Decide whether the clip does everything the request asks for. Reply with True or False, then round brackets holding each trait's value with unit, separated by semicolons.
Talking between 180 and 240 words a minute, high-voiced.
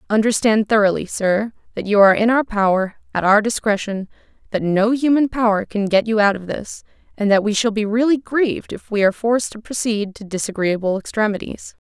True (190 wpm; 215 Hz)